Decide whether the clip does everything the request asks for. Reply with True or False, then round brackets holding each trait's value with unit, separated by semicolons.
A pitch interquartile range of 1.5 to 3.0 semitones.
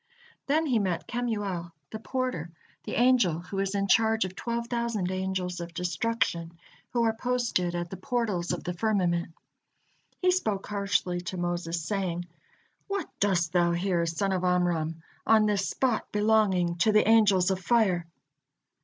False (4.2 semitones)